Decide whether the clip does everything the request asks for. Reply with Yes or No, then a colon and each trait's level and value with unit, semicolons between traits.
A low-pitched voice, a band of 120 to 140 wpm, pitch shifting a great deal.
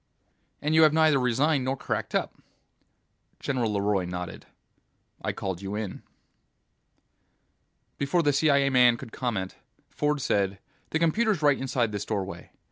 Yes: low, 130 Hz; slow, 135 wpm; wide, 6.3 semitones